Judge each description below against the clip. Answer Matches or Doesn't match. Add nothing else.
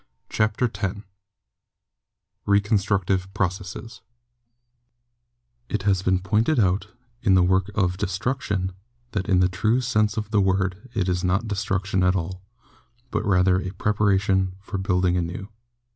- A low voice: Matches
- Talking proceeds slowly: Matches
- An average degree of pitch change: Doesn't match